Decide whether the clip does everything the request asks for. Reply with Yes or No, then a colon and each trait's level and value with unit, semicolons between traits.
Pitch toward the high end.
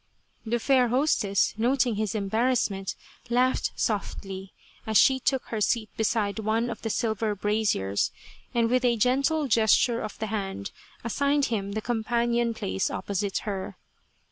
Yes: high, 220 Hz